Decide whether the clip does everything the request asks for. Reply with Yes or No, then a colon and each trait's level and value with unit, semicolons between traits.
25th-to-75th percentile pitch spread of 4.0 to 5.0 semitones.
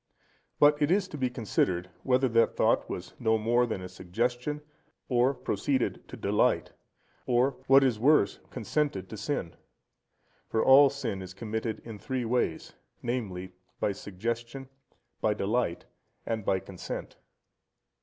Yes: average, 4.6 semitones